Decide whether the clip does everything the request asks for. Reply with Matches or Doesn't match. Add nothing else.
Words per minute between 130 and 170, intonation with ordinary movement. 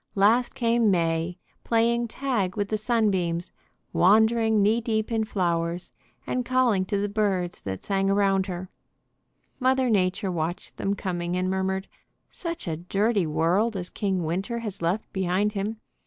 Matches